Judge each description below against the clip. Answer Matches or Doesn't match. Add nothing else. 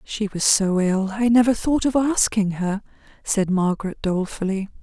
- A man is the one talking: Doesn't match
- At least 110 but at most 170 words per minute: Matches